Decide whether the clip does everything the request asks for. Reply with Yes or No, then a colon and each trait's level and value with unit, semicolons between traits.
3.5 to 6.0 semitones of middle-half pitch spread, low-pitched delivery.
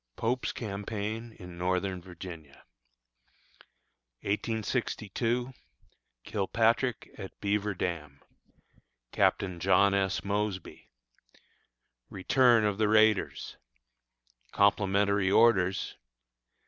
No: average, 2.8 semitones; low, 100 Hz